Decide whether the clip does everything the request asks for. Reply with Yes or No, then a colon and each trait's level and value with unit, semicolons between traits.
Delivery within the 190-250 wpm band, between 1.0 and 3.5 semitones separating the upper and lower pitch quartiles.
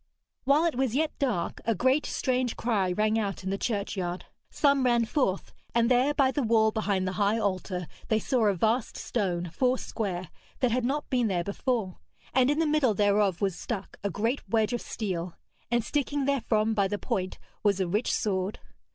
No: average, 195 wpm; average, 4.5 semitones